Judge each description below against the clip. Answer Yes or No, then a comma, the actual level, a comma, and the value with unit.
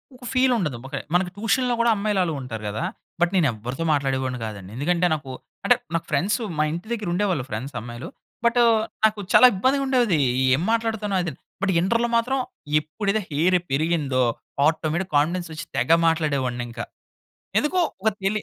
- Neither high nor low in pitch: Yes, medium, 170 Hz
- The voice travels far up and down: Yes, wide, 7.7 semitones